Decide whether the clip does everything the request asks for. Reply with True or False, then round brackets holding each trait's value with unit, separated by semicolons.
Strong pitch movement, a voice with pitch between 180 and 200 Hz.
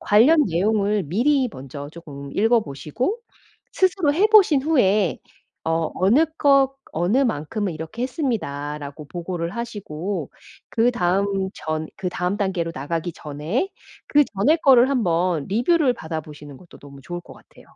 True (7.8 semitones; 190 Hz)